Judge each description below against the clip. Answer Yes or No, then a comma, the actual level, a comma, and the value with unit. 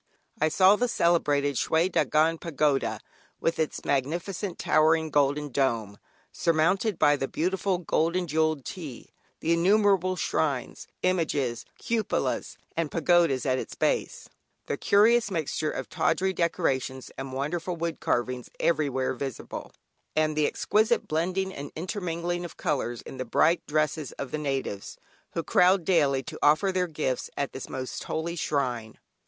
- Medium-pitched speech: Yes, medium, 155 Hz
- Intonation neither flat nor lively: Yes, average, 4.2 semitones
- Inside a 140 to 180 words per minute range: Yes, average, 145 wpm